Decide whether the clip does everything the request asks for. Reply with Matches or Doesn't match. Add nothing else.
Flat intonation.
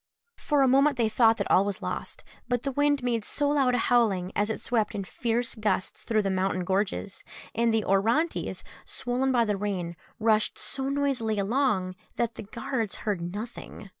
Doesn't match